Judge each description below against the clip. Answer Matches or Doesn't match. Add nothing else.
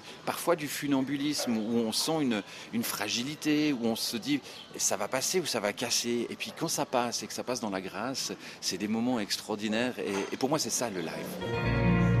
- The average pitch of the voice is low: Matches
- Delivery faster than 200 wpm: Matches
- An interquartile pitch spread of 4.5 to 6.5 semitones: Matches